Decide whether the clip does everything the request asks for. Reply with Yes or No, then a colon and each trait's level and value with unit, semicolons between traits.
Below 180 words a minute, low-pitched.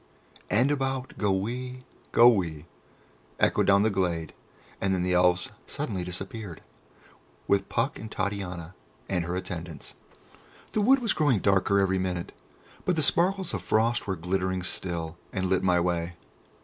Yes: average, 150 wpm; very low, 95 Hz